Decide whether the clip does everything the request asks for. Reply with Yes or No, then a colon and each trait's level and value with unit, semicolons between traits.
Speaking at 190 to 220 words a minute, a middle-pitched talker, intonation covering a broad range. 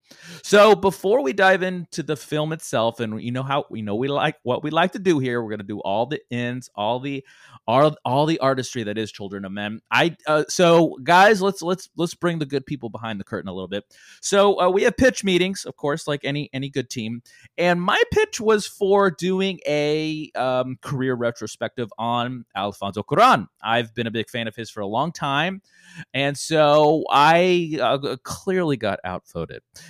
Yes: fast, 205 wpm; medium, 145 Hz; wide, 6.8 semitones